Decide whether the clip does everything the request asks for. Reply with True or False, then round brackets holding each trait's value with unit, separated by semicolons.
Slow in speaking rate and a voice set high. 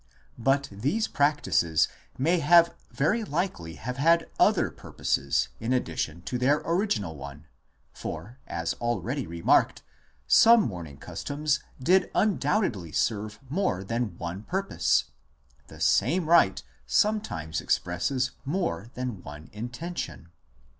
False (115 wpm; 125 Hz)